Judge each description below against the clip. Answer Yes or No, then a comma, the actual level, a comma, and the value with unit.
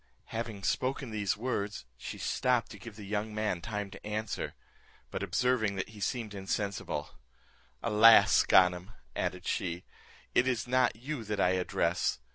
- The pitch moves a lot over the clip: No, average, 2.9 semitones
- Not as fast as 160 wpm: Yes, average, 150 wpm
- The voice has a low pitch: Yes, low, 105 Hz